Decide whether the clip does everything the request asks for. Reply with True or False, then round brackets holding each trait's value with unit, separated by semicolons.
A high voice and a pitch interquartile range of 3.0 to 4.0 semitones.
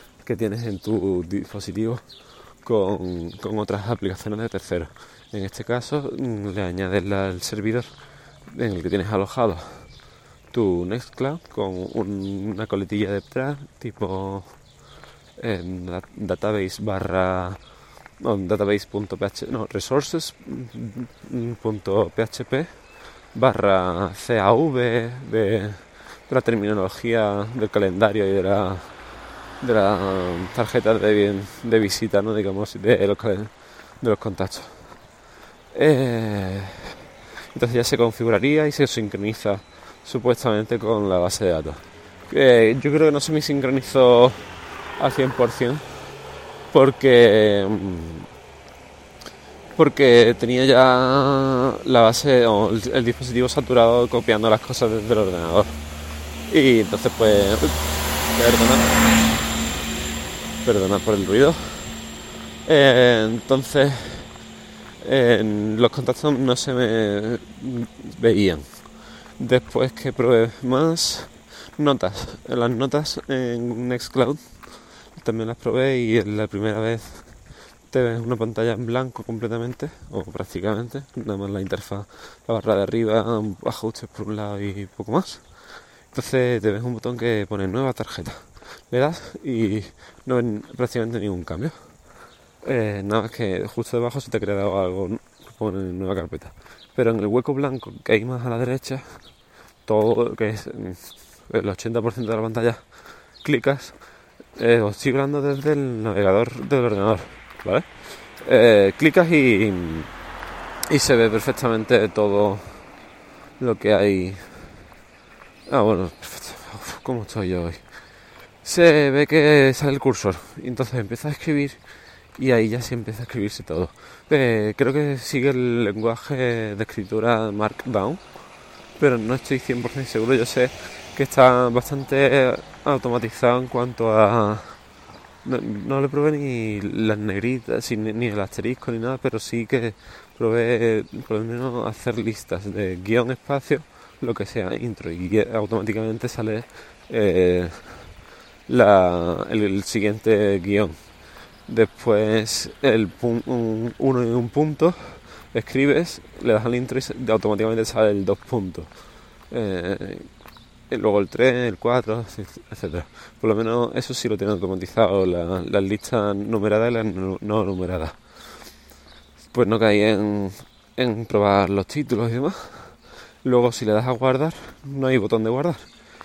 False (110 Hz; 3.6 semitones)